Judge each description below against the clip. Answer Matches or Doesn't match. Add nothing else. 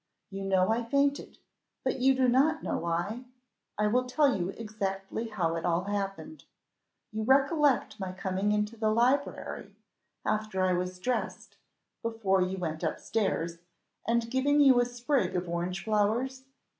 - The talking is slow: Doesn't match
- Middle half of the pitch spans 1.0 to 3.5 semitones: Doesn't match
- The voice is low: Doesn't match